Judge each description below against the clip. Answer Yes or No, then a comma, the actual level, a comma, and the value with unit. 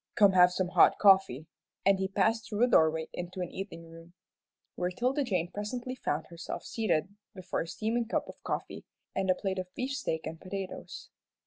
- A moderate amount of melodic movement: Yes, average, 3.8 semitones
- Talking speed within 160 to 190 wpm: Yes, average, 185 wpm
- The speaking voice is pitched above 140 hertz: Yes, high, 190 Hz